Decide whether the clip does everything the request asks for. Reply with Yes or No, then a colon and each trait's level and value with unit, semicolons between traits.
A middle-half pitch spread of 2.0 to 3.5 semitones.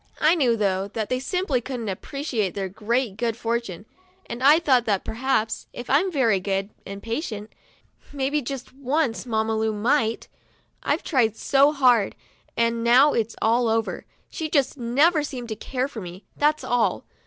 No: average, 3.9 semitones